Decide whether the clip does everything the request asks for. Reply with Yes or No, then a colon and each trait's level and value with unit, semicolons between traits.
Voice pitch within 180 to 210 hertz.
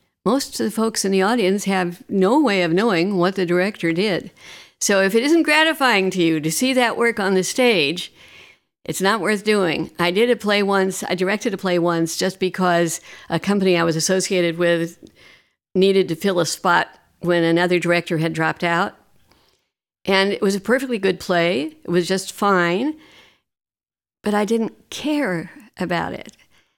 Yes: high, 190 Hz